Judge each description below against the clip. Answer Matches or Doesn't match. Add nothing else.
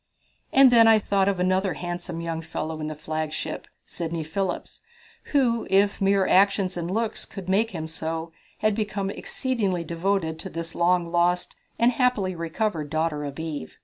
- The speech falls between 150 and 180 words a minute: Matches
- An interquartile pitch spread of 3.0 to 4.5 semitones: Matches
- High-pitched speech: Doesn't match